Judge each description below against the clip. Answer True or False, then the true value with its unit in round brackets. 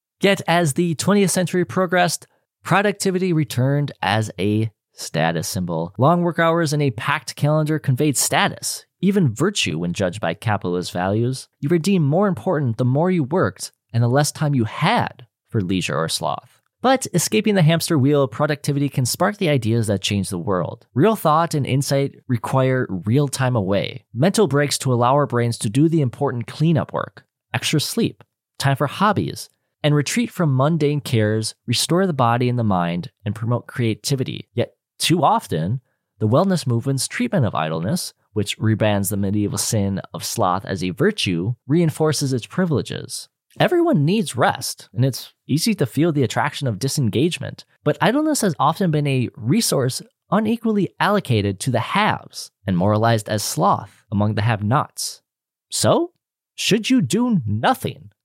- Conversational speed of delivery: True (165 wpm)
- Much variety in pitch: True (6.9 semitones)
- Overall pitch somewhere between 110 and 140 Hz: True (135 Hz)